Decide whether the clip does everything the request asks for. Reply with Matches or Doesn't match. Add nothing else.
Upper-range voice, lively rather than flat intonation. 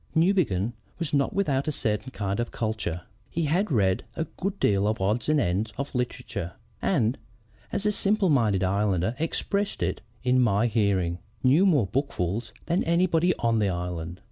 Doesn't match